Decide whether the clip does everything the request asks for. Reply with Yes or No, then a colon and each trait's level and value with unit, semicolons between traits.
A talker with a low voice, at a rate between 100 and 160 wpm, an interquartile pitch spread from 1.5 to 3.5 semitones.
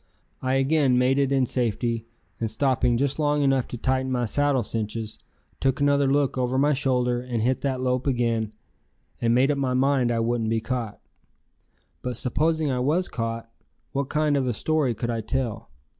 No: low, 130 Hz; average, 185 wpm; average, 2.9 semitones